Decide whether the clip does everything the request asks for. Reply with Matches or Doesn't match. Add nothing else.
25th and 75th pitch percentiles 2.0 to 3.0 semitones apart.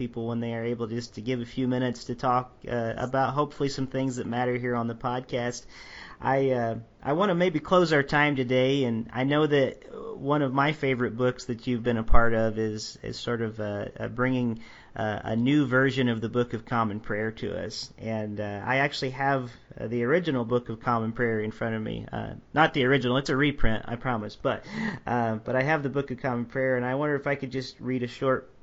Matches